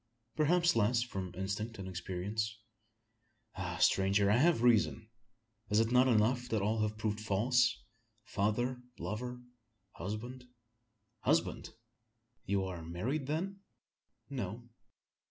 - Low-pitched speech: Yes, low, 110 Hz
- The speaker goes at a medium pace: No, slow, 115 wpm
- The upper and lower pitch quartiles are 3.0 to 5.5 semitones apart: Yes, average, 3.7 semitones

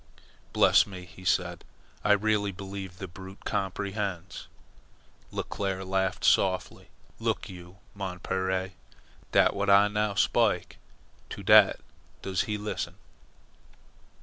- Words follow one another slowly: Yes, slow, 115 wpm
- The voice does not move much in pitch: Yes, narrow, 1.5 semitones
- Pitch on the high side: No, very low, 95 Hz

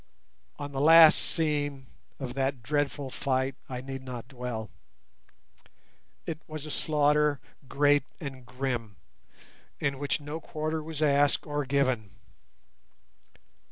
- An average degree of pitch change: No, narrow, 2.3 semitones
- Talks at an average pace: No, slow, 120 wpm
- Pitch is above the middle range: No, medium, 140 Hz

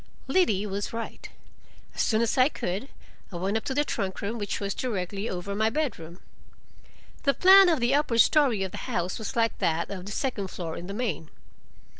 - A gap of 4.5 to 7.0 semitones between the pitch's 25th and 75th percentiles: Yes, average, 5.2 semitones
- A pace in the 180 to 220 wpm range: Yes, average, 200 wpm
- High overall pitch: Yes, high, 215 Hz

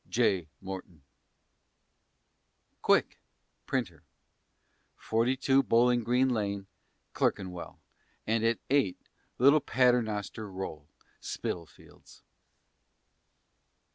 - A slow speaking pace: Yes, slow, 70 wpm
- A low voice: Yes, low, 110 Hz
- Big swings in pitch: No, average, 4.6 semitones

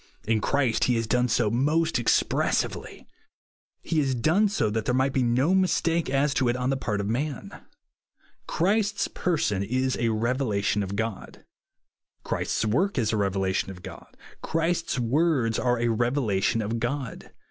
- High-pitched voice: No, low, 125 Hz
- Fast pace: No, average, 160 wpm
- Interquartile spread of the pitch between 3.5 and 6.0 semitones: Yes, average, 4.7 semitones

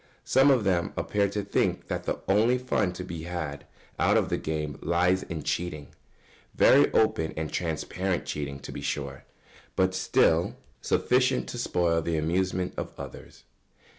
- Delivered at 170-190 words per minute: No, average, 160 wpm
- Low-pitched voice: Yes, very low, 90 Hz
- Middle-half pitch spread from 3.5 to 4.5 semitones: Yes, average, 4.1 semitones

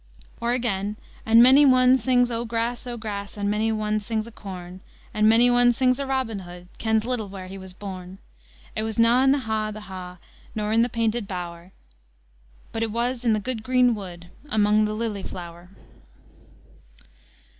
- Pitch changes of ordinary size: Yes, average, 3.4 semitones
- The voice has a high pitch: Yes, high, 220 Hz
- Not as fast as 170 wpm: No, average, 185 wpm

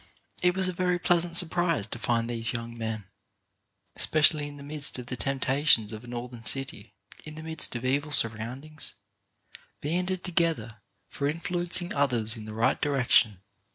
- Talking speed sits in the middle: Yes, average, 170 wpm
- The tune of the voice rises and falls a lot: Yes, wide, 5.8 semitones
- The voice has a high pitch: No, medium, 140 Hz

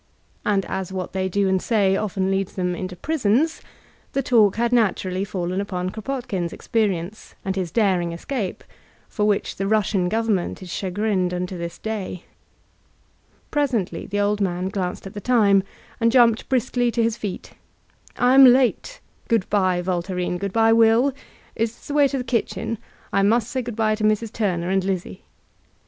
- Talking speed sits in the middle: Yes, average, 170 wpm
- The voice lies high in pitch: Yes, high, 205 Hz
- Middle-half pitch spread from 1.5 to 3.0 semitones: No, average, 3.6 semitones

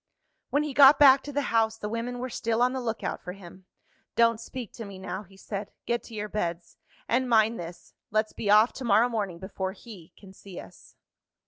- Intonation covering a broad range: No, average, 4.0 semitones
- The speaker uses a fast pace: Yes, fast, 220 wpm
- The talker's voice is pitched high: Yes, high, 220 Hz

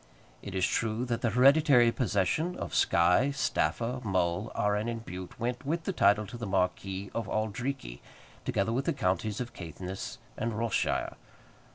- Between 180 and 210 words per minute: No, average, 165 wpm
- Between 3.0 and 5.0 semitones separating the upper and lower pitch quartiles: Yes, average, 4.4 semitones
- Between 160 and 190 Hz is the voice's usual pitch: No, low, 110 Hz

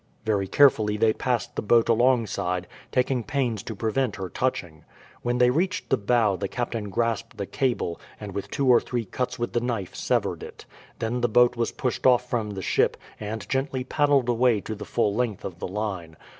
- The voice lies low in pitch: Yes, low, 115 Hz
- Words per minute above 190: Yes, average, 200 wpm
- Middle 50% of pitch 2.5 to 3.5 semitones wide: Yes, average, 3.1 semitones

